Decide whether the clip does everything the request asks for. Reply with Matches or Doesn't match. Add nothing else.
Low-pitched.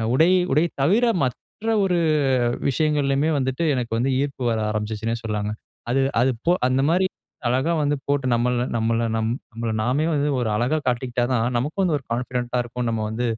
Matches